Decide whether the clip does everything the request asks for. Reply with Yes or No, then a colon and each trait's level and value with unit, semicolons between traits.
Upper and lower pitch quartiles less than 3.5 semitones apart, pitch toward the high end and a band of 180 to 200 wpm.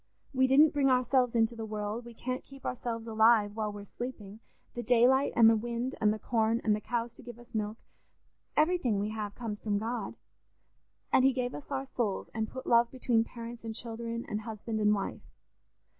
Yes: narrow, 2.4 semitones; high, 230 Hz; average, 195 wpm